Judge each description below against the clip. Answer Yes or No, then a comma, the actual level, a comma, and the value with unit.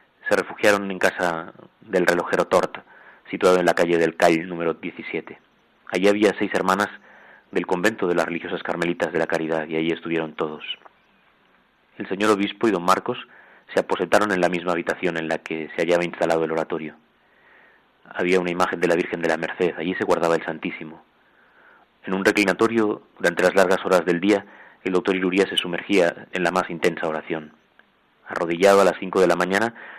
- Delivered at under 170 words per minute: No, average, 185 wpm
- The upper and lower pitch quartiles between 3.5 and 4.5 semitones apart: No, average, 2.7 semitones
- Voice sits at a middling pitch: No, very low, 85 Hz